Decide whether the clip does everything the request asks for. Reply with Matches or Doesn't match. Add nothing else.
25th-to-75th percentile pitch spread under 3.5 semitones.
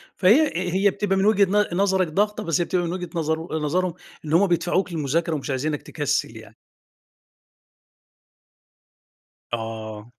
Doesn't match